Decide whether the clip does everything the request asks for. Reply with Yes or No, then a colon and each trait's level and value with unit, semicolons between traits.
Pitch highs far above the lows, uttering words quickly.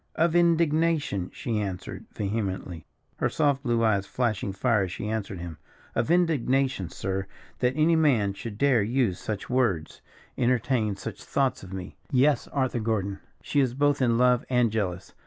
No: wide, 5.7 semitones; average, 160 wpm